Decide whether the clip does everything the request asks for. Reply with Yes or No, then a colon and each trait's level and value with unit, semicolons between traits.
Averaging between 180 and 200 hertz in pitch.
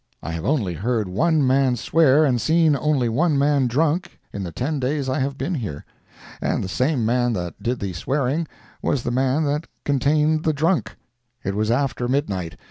No: low, 130 Hz